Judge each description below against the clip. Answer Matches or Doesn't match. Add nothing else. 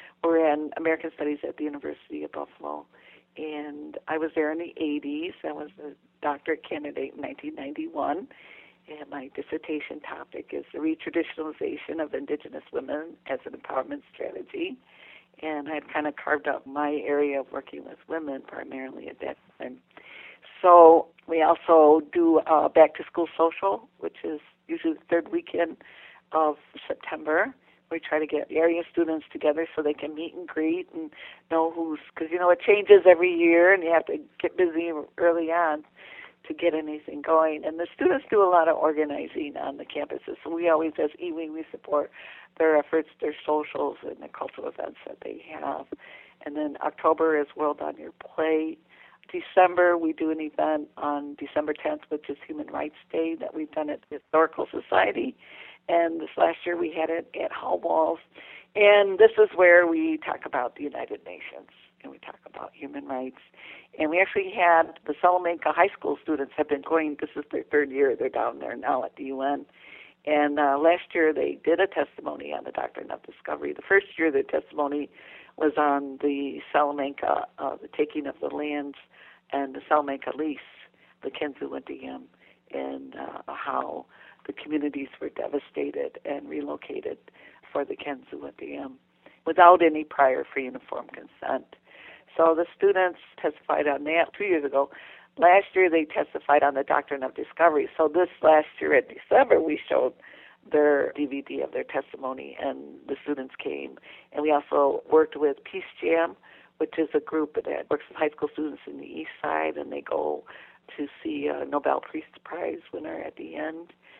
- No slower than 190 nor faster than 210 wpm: Doesn't match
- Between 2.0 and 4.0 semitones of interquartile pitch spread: Matches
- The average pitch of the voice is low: Doesn't match